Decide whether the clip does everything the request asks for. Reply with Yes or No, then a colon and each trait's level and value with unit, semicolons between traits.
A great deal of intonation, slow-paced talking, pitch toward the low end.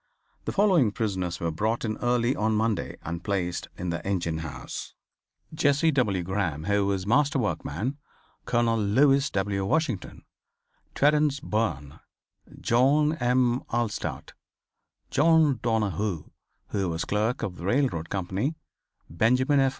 Yes: wide, 6.0 semitones; slow, 125 wpm; low, 110 Hz